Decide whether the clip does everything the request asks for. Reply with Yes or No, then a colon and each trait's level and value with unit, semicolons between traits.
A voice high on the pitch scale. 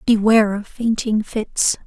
Yes: high, 215 Hz